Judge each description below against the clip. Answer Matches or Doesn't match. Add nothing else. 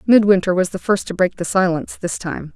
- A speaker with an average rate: Doesn't match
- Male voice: Doesn't match